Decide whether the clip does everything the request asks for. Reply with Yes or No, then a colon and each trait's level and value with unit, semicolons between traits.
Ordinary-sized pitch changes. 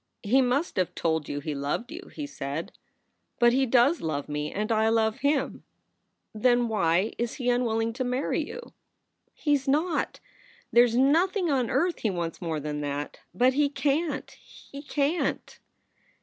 No: wide, 8.2 semitones